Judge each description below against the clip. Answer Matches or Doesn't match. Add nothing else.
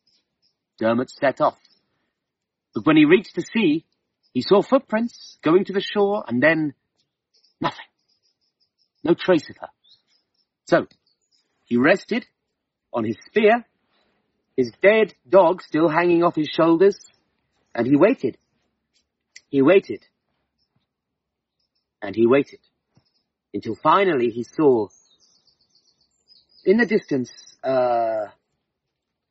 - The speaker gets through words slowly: Matches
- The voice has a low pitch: Doesn't match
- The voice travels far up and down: Matches